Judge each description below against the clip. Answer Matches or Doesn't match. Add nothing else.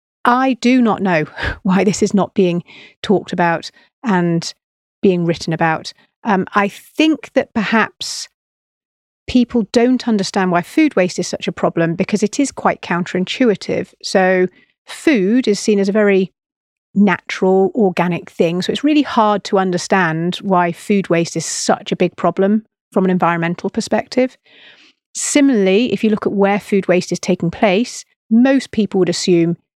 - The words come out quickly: Doesn't match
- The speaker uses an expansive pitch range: Doesn't match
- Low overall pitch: Doesn't match